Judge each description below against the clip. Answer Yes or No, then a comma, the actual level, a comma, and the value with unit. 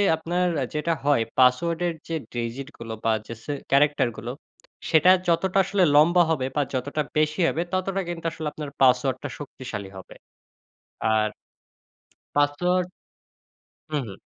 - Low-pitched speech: No, medium, 145 Hz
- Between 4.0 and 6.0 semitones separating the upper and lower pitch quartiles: Yes, average, 4.9 semitones